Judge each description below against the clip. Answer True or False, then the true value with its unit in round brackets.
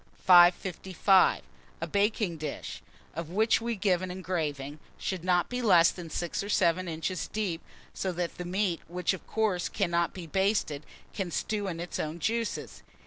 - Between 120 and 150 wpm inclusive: False (165 wpm)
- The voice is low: False (180 Hz)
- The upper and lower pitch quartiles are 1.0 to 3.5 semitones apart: True (2.8 semitones)